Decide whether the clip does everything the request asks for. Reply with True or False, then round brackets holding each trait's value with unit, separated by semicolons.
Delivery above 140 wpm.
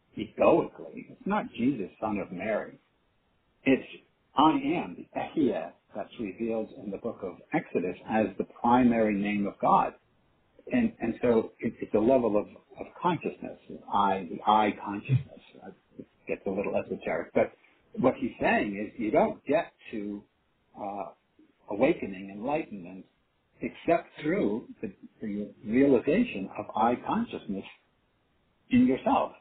False (135 wpm)